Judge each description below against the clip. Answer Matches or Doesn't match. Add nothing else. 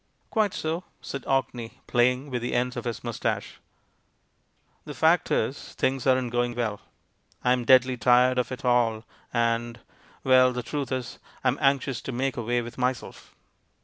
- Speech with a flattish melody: Matches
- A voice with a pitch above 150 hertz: Doesn't match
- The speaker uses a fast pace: Doesn't match